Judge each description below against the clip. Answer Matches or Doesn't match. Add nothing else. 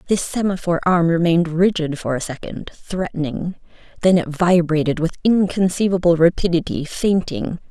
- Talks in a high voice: Doesn't match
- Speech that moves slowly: Matches